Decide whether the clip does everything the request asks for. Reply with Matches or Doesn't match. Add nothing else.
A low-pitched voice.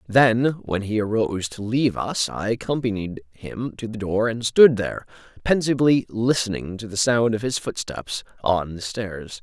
Matches